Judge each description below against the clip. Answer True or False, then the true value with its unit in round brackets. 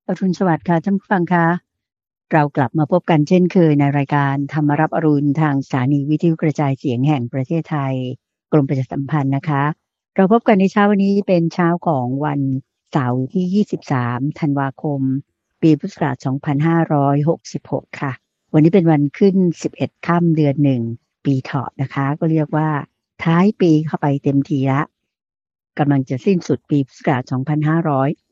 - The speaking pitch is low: False (150 Hz)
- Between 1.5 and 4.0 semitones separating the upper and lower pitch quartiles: True (3.4 semitones)